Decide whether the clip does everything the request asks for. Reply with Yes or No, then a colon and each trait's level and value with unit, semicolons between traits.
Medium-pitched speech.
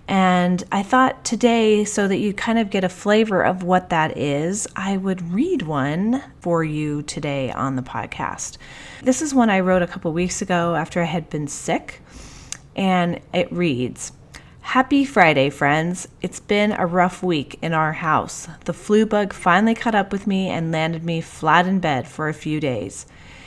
Yes: medium, 180 Hz